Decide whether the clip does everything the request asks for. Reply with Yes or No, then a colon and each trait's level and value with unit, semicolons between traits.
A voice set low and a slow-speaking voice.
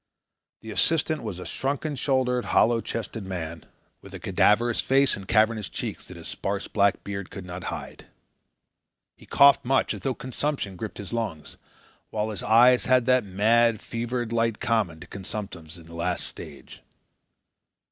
No: low, 110 Hz; average, 160 wpm